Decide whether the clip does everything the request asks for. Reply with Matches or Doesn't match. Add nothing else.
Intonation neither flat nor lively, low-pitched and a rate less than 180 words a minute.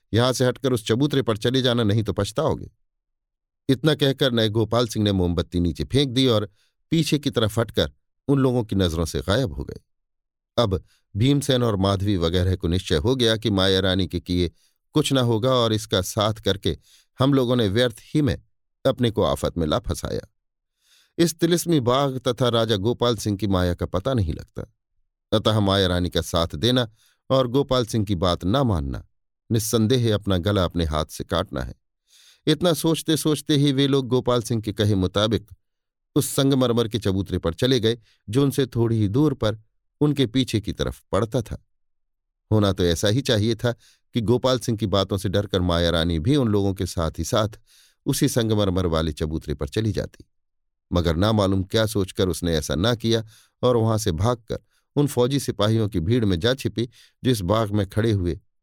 Doesn't match